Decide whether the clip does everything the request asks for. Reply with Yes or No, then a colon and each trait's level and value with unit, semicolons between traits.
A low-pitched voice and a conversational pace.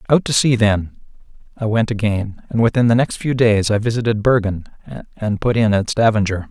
Yes: low, 110 Hz; average, 195 wpm